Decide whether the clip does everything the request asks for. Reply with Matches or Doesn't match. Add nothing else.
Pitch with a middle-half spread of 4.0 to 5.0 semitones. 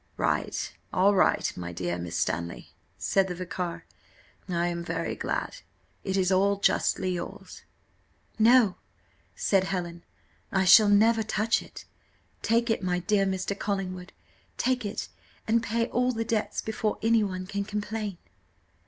Doesn't match